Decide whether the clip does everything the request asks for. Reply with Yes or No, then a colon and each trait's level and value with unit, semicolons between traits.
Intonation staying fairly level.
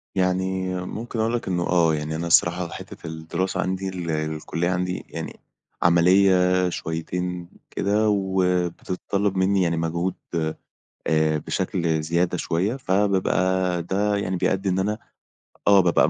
Yes: narrow, 2.0 semitones